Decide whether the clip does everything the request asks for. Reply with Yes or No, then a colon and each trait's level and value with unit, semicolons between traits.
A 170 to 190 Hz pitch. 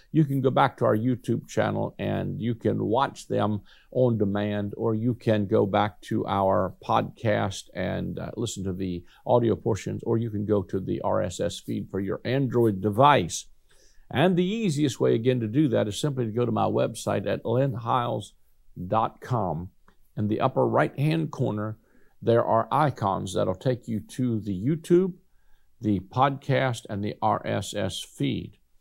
No: low, 115 Hz